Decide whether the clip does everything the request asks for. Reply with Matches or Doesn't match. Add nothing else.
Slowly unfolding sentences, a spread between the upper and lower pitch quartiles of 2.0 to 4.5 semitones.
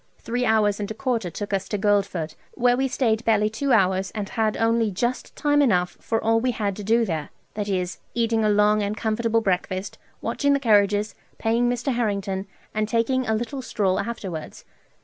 Doesn't match